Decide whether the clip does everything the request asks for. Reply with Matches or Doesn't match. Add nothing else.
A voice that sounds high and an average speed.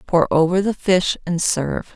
Doesn't match